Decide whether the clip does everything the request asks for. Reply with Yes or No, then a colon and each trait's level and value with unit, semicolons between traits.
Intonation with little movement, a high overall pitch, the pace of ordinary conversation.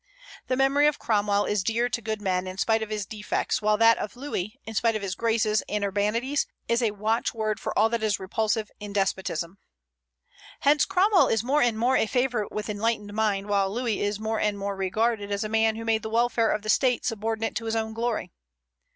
No: narrow, 2.1 semitones; high, 220 Hz; fast, 215 wpm